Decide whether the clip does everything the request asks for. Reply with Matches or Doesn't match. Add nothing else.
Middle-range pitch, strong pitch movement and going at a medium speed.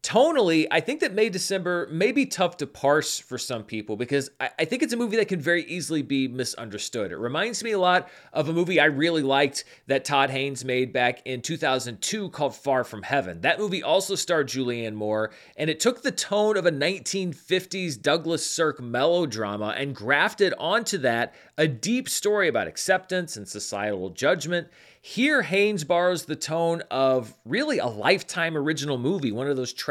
Matches